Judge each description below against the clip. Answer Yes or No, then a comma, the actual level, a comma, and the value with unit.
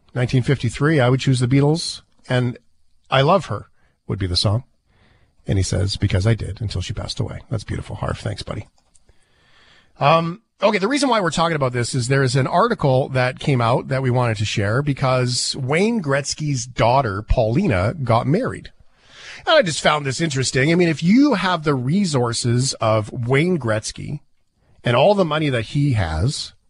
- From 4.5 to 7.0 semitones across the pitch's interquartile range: Yes, average, 4.9 semitones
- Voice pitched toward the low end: Yes, low, 130 Hz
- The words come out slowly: No, average, 180 wpm